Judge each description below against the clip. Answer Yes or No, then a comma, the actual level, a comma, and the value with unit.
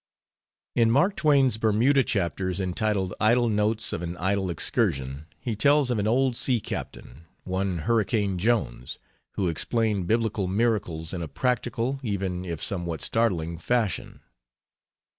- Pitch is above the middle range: No, low, 105 Hz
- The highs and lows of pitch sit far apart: No, average, 4.7 semitones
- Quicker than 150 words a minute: No, slow, 135 wpm